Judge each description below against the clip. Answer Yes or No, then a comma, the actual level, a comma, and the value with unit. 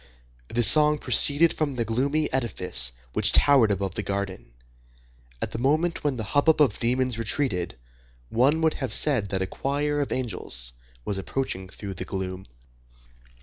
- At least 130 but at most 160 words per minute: Yes, average, 155 wpm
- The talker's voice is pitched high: No, low, 120 Hz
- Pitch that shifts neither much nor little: No, wide, 6.8 semitones